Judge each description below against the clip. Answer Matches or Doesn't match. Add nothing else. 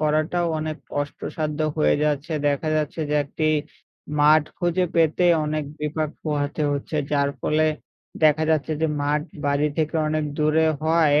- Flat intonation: Matches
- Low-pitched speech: Doesn't match